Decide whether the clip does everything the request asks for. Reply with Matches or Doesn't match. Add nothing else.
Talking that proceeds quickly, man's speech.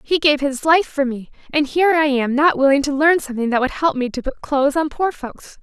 Doesn't match